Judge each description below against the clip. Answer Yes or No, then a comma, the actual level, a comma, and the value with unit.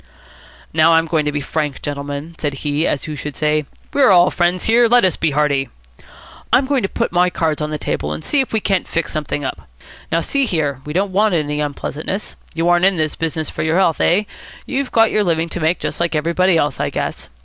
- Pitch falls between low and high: Yes, medium, 165 Hz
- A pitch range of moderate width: Yes, average, 3.9 semitones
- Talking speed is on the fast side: Yes, fast, 230 wpm